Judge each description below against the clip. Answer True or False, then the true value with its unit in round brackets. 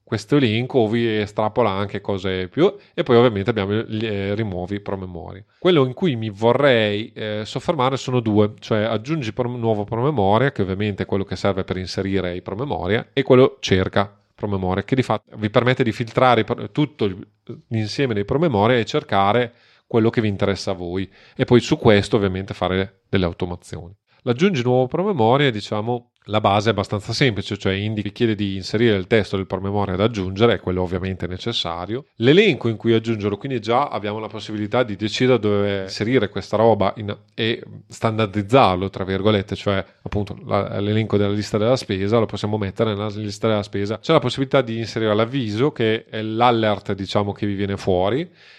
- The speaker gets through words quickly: True (180 wpm)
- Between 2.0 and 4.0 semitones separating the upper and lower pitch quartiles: True (3.3 semitones)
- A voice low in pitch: True (110 Hz)